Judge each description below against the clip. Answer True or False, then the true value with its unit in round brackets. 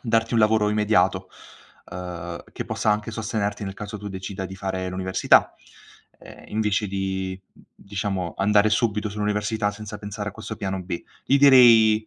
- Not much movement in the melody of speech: True (2.1 semitones)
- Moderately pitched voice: False (105 Hz)